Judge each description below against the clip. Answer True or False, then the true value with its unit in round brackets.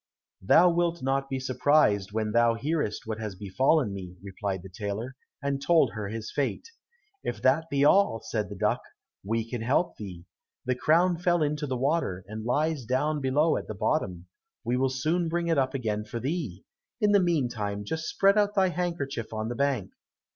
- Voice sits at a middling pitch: False (130 Hz)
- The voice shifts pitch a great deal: True (6.7 semitones)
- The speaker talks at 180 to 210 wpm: True (190 wpm)